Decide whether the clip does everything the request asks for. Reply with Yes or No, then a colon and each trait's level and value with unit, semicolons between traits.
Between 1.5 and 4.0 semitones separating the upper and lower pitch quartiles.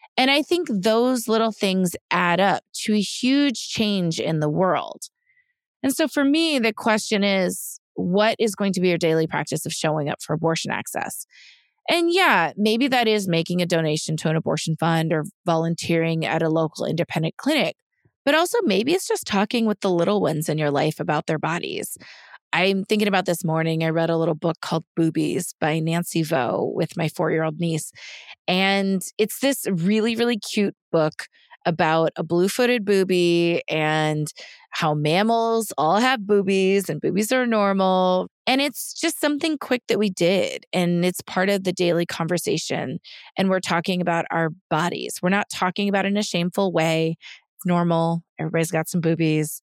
No: average, 4.8 semitones